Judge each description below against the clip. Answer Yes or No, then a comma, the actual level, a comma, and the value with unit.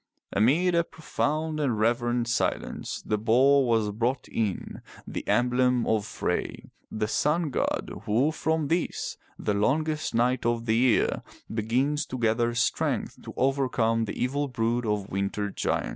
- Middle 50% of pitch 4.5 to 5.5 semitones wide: No, average, 4.0 semitones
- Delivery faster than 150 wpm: No, average, 145 wpm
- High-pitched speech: No, low, 120 Hz